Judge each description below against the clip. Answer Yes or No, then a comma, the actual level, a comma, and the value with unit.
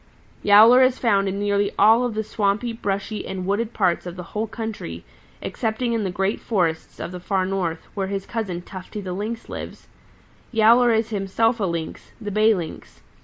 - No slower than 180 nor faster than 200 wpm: Yes, average, 185 wpm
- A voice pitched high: Yes, high, 205 Hz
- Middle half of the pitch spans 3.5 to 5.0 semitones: No, average, 2.9 semitones